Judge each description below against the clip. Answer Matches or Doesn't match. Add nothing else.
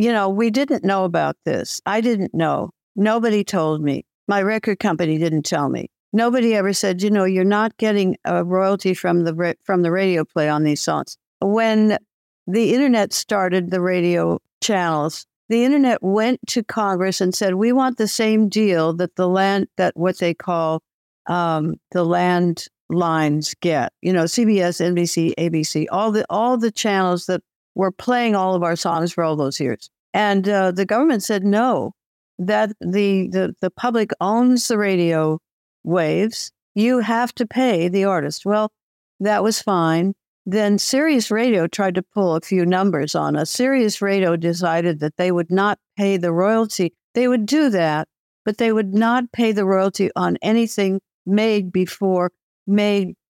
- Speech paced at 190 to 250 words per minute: Doesn't match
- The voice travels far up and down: Doesn't match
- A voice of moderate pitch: Doesn't match